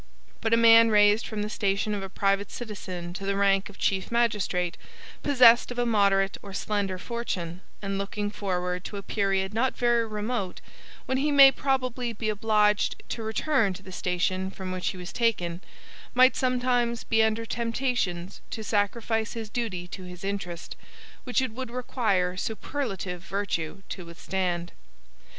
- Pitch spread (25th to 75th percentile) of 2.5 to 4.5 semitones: Yes, average, 3.6 semitones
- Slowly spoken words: No, average, 165 wpm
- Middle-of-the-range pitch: No, high, 205 Hz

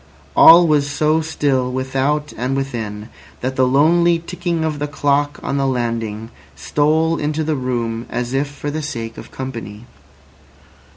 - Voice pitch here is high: No, medium, 140 Hz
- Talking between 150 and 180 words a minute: Yes, average, 155 wpm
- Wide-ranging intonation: No, average, 3.7 semitones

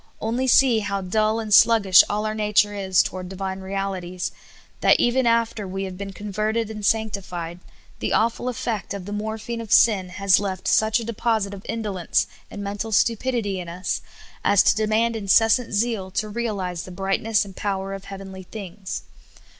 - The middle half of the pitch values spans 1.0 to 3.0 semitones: Yes, narrow, 2.6 semitones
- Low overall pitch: No, high, 205 Hz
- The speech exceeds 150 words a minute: Yes, average, 180 wpm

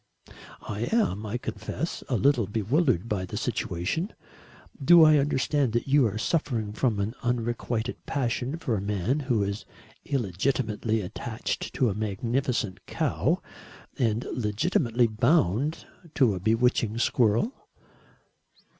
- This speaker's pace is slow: Yes, slow, 125 wpm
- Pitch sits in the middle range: No, low, 115 Hz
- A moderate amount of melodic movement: Yes, average, 4.1 semitones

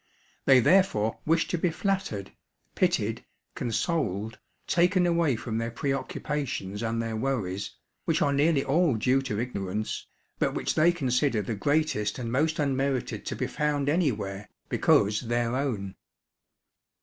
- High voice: No, low, 130 Hz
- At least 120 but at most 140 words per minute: Yes, slow, 135 wpm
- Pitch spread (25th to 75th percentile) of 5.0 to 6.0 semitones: Yes, wide, 5.6 semitones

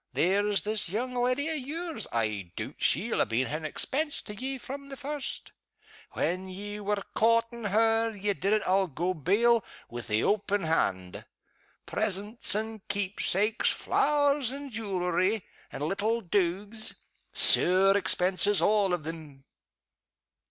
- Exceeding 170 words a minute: No, average, 140 wpm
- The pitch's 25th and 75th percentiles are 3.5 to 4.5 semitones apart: Yes, average, 4.2 semitones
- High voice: Yes, high, 205 Hz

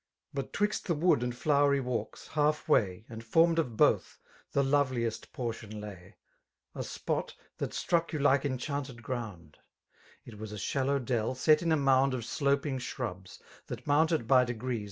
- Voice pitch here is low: Yes, low, 130 Hz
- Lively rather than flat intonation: No, average, 4.0 semitones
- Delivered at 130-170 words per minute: Yes, average, 165 wpm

